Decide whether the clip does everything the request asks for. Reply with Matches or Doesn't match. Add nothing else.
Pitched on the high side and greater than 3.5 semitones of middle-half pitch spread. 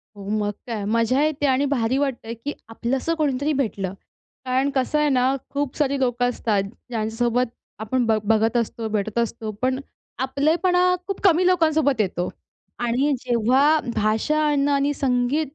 Matches